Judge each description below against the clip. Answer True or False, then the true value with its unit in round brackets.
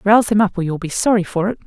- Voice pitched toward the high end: True (200 Hz)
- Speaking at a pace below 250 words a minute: False (325 wpm)